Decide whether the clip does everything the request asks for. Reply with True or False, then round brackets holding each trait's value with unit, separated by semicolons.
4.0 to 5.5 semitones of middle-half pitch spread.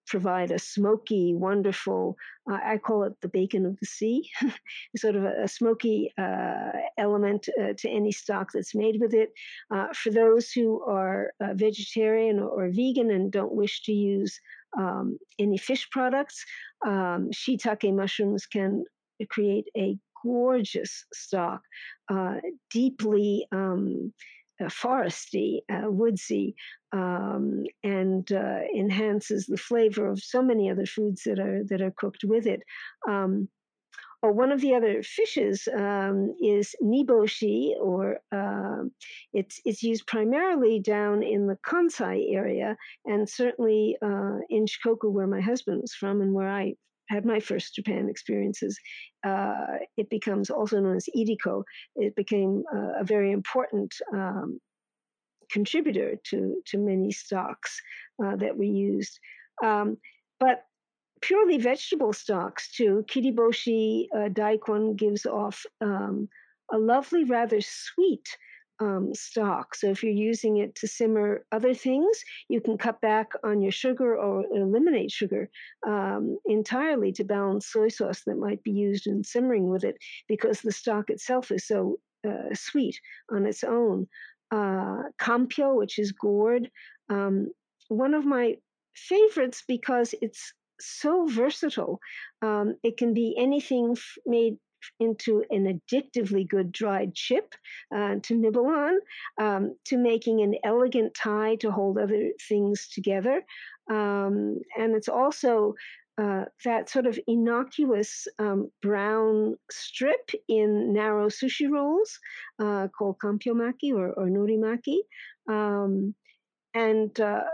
False (3.1 semitones)